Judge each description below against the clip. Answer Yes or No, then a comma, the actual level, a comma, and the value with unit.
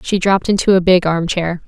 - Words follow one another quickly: Yes, fast, 250 wpm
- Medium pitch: Yes, medium, 180 Hz